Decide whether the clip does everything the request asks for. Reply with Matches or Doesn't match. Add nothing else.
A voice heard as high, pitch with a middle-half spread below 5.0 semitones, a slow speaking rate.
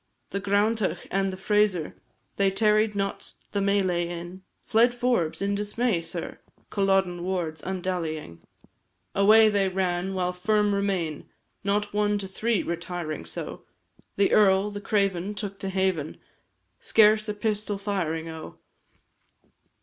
Matches